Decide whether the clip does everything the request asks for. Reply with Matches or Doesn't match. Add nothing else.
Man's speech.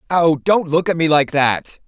Matches